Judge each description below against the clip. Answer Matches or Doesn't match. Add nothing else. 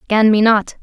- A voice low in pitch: Doesn't match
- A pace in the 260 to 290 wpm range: Doesn't match